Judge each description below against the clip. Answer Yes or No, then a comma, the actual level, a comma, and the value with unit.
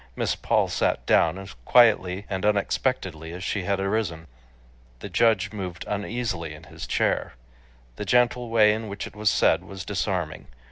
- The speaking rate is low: No, average, 160 wpm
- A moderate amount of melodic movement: Yes, average, 3.2 semitones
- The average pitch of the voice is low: Yes, low, 100 Hz